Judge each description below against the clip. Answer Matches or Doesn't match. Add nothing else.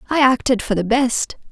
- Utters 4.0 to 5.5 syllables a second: Matches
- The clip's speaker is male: Doesn't match